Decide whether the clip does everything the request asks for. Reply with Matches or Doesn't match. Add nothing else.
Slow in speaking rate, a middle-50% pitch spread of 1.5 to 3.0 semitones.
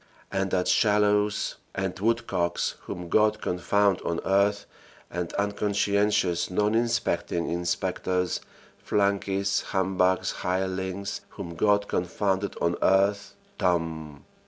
Matches